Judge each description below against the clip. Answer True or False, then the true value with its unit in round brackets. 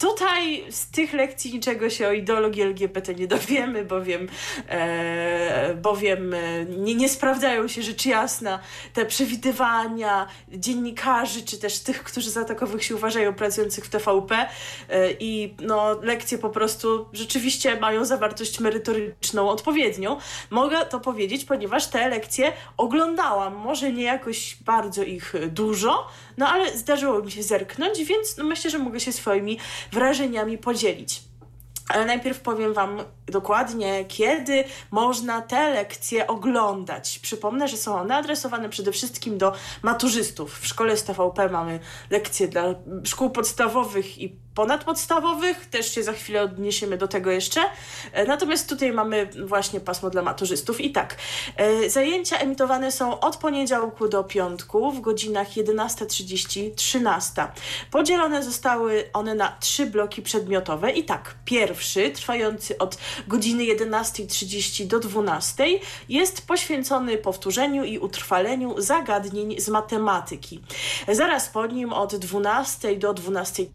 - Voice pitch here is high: True (220 Hz)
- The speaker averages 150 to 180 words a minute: False (130 wpm)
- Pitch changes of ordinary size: True (4.3 semitones)